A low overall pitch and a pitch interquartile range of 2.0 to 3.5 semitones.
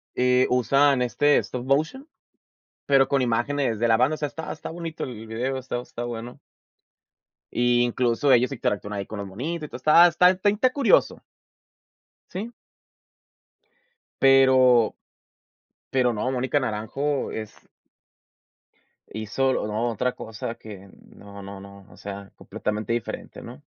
No: low, 125 Hz; average, 4.1 semitones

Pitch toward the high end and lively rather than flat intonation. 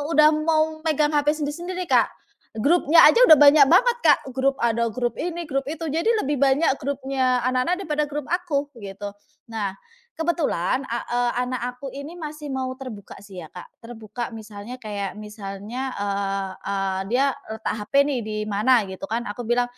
Yes: very high, 255 Hz; wide, 5.7 semitones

